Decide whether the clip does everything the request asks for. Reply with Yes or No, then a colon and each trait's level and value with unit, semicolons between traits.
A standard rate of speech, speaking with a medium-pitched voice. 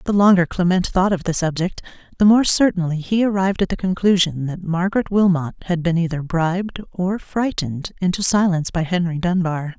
Yes: average, 180 wpm; medium, 180 Hz